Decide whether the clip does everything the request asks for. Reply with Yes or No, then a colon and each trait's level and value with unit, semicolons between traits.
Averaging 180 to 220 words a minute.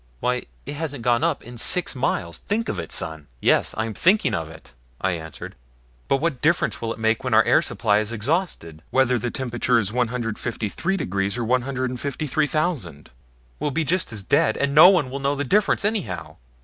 Yes: average, 190 wpm